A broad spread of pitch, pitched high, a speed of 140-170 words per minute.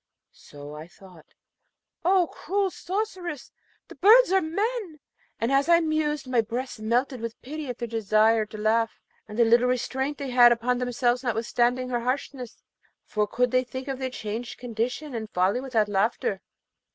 No: average, 4.0 semitones; high, 245 Hz; average, 165 wpm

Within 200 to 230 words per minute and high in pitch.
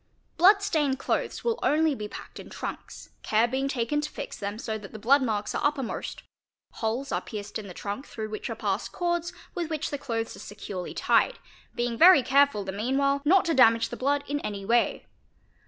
Yes: fast, 205 wpm; very high, 260 Hz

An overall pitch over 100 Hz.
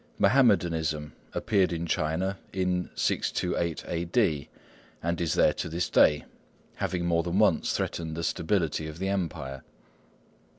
No: very low, 85 Hz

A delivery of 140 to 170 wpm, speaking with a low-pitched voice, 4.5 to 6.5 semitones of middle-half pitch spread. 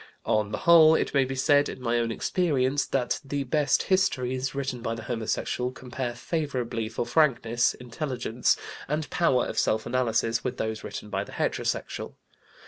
No: average, 165 wpm; low, 125 Hz; average, 3.4 semitones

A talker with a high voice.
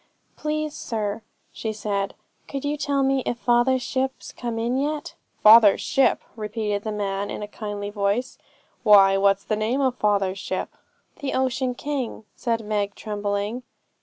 Yes: high, 225 Hz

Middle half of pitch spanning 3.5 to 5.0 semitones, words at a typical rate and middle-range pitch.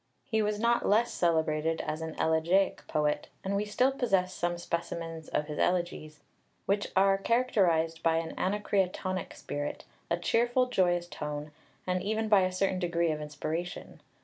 Yes: average, 3.8 semitones; average, 155 wpm; medium, 180 Hz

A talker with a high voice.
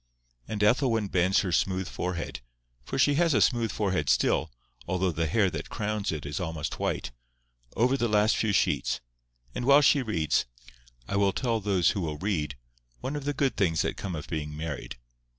No: very low, 95 Hz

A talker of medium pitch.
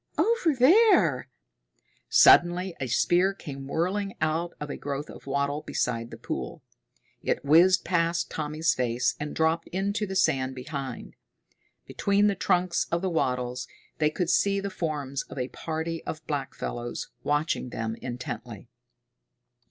Yes: medium, 160 Hz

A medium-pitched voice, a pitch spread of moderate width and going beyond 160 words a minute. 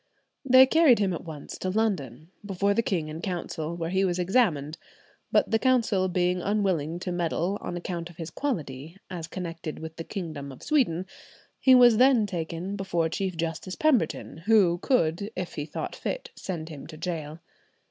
Yes: medium, 180 Hz; average, 4.0 semitones; average, 180 wpm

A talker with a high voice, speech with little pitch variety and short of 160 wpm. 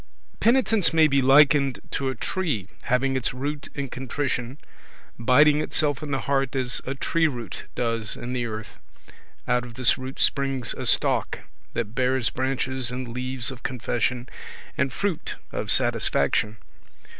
No: low, 130 Hz; narrow, 2.2 semitones; average, 150 wpm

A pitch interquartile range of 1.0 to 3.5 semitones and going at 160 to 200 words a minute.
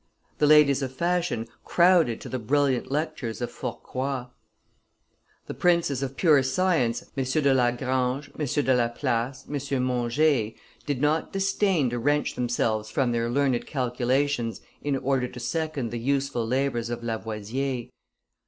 No: average, 3.2 semitones; average, 140 wpm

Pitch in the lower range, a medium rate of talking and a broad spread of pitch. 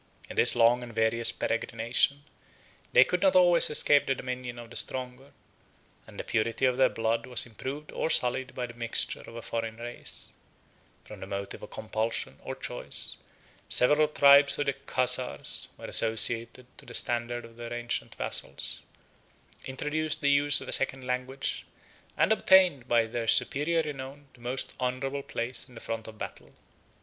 No: low, 125 Hz; average, 170 wpm; average, 3.1 semitones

